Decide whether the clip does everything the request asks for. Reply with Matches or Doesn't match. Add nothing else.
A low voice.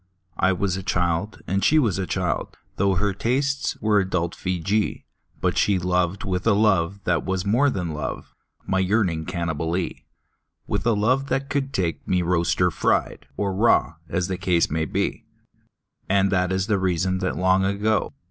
Matches